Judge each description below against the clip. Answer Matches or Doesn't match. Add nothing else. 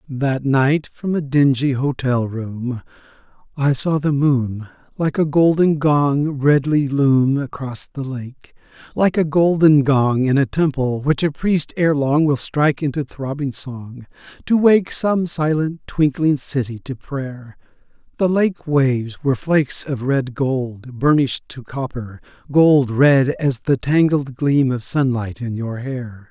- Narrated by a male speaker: Matches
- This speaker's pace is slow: Doesn't match